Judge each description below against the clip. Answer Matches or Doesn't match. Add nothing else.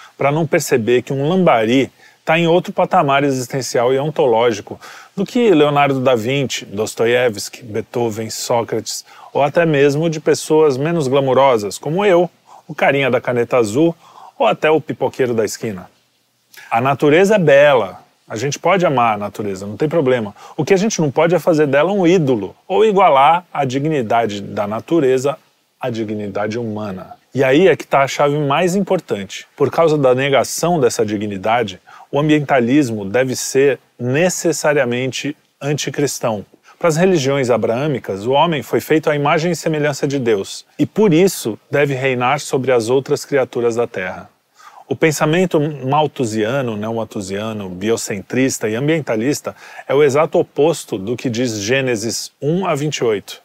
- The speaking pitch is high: Doesn't match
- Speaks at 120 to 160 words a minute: Matches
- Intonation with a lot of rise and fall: Doesn't match